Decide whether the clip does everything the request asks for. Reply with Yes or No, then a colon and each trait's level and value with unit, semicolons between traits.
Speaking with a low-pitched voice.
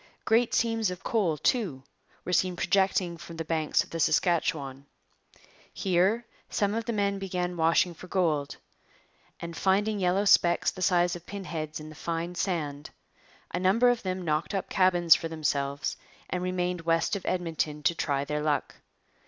No: medium, 175 Hz